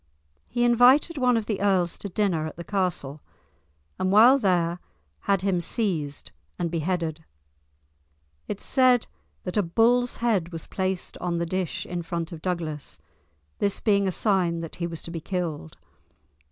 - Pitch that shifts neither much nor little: Yes, average, 3.8 semitones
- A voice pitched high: No, medium, 180 Hz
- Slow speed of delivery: No, average, 165 wpm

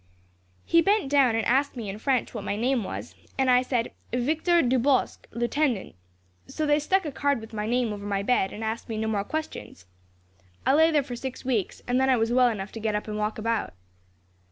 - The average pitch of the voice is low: No, high, 245 Hz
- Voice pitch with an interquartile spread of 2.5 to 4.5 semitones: Yes, average, 4.1 semitones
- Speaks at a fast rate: Yes, fast, 220 wpm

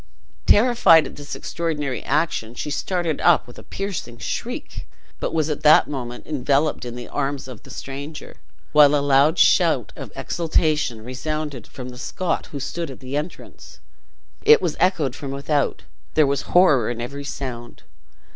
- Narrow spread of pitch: No, average, 3.3 semitones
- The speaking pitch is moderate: Yes, medium, 145 Hz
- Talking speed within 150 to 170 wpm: Yes, average, 165 wpm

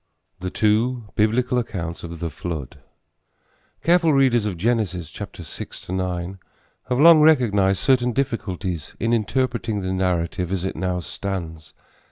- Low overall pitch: Yes, low, 100 Hz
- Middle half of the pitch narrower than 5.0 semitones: No, average, 5.3 semitones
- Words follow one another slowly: Yes, slow, 130 wpm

